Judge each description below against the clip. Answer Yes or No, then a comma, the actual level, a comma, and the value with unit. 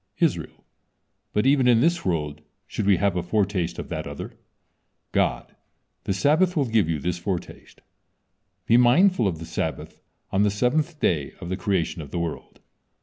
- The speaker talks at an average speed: Yes, average, 170 wpm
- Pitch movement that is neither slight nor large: No, wide, 6.3 semitones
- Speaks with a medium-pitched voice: No, low, 100 Hz